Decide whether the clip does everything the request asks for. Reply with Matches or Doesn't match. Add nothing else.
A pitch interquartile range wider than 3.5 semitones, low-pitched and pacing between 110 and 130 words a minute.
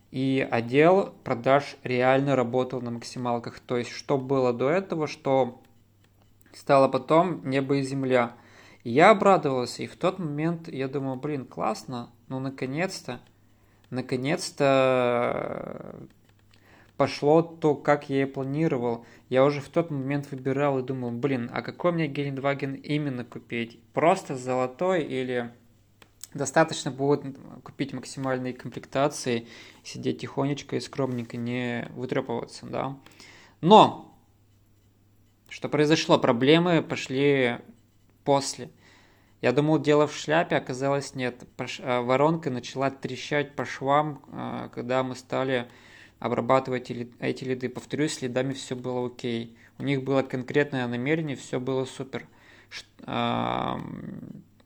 Doesn't match